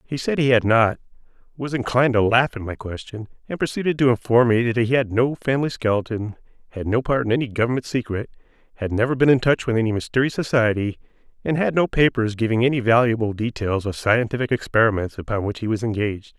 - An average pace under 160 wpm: No, average, 200 wpm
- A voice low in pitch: Yes, low, 115 Hz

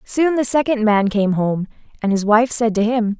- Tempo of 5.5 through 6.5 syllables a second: No, 4.7 syllables/s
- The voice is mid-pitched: No, high, 225 Hz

